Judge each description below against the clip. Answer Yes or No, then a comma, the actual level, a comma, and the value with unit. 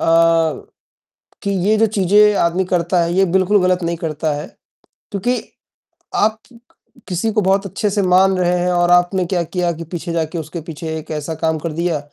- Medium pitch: Yes, medium, 180 Hz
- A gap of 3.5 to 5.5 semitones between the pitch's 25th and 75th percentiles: No, narrow, 2.4 semitones